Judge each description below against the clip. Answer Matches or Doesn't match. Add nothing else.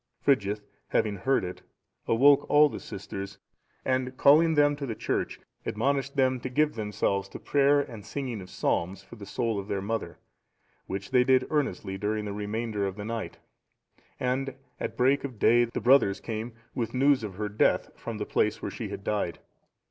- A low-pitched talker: Matches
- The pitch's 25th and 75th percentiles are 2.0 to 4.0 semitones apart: Doesn't match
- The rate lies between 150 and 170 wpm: Doesn't match